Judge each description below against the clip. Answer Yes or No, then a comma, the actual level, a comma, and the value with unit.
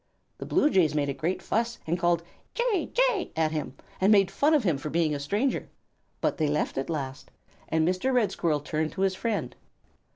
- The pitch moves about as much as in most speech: No, wide, 6.9 semitones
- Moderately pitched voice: Yes, medium, 175 Hz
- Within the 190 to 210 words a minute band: Yes, fast, 205 wpm